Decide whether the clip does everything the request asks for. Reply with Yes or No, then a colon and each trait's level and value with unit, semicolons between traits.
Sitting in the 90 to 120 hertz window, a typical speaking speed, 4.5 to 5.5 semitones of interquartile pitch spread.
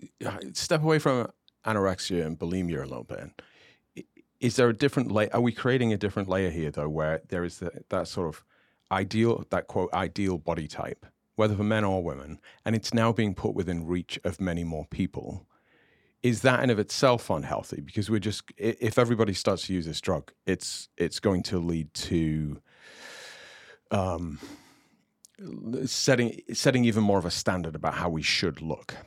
Yes: low, 100 Hz; average, 175 wpm; average, 5.0 semitones